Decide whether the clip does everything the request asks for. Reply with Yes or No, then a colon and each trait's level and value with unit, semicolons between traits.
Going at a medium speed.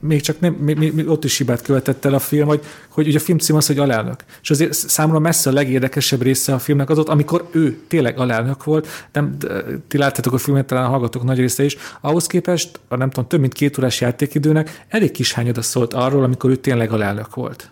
No: fast, 235 wpm